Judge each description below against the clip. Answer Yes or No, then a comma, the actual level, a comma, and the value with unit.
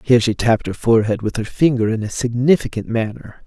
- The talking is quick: Yes, fast, 210 wpm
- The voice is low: Yes, low, 115 Hz